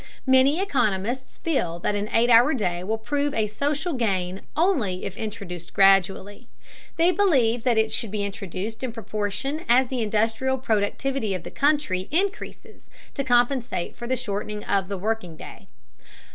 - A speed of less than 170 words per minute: Yes, average, 160 wpm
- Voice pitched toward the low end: No, high, 225 Hz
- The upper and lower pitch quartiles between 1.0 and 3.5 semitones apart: No, average, 4.7 semitones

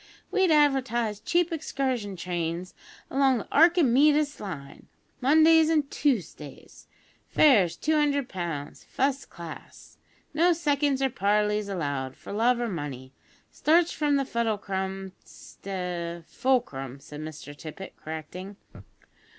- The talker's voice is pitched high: Yes, high, 215 Hz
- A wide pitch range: Yes, wide, 8.8 semitones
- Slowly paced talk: Yes, slow, 120 wpm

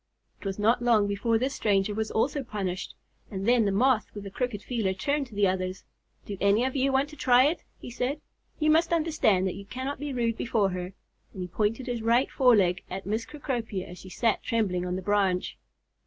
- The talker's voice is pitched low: No, high, 220 Hz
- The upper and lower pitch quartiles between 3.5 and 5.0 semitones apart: Yes, average, 4.7 semitones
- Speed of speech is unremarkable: No, fast, 220 wpm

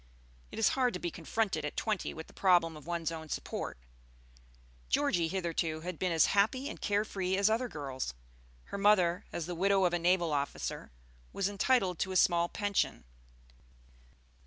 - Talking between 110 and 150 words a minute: No, average, 175 wpm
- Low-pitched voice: No, medium, 180 Hz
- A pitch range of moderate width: Yes, average, 3.4 semitones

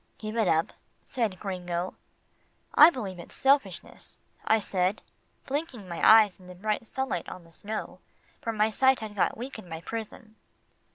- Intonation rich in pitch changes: No, average, 4.0 semitones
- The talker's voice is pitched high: Yes, high, 215 Hz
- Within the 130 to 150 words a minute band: No, average, 165 wpm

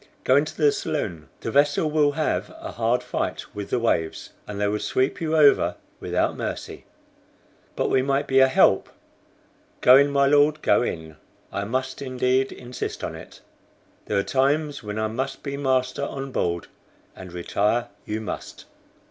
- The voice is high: No, low, 130 Hz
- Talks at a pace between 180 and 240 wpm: No, average, 170 wpm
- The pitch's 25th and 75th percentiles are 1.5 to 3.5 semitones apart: No, average, 4.7 semitones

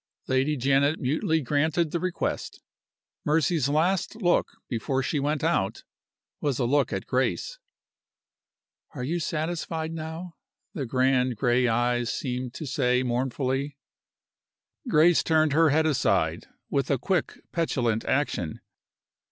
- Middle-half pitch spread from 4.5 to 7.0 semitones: No, average, 4.0 semitones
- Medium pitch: Yes, medium, 145 Hz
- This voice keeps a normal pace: No, slow, 125 wpm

